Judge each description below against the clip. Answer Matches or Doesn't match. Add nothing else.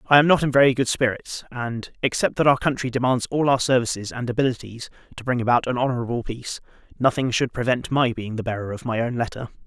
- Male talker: Matches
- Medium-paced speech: Doesn't match